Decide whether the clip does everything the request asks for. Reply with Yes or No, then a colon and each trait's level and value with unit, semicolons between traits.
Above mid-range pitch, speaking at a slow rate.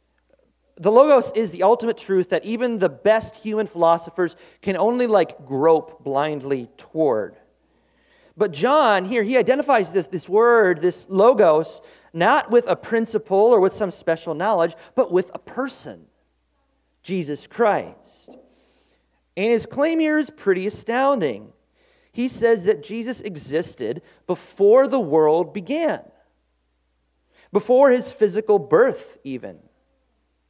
Yes: high, 205 Hz; slow, 125 wpm